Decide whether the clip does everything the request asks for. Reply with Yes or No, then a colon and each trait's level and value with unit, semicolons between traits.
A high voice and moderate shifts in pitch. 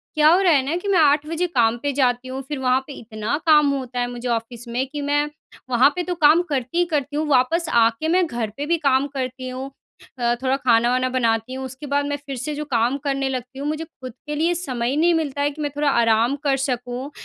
Yes: very high, 270 Hz; average, 3.3 semitones